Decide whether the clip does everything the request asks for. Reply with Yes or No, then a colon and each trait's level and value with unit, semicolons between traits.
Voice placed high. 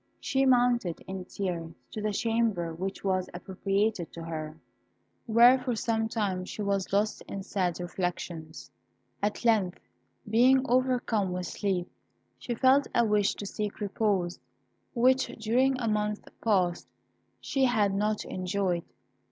Yes: high, 205 Hz